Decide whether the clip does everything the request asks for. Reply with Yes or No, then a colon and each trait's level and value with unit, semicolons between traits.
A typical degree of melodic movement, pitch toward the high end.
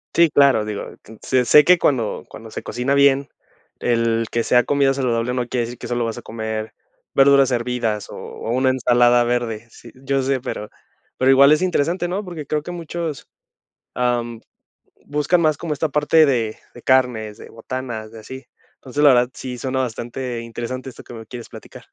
No: average, 3.1 semitones; low, 125 Hz